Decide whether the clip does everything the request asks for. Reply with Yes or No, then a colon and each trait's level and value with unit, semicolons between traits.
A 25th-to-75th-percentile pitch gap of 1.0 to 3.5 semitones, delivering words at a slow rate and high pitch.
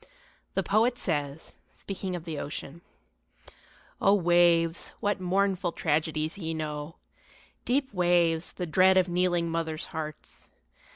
No: average, 2.9 semitones; slow, 120 wpm; medium, 175 Hz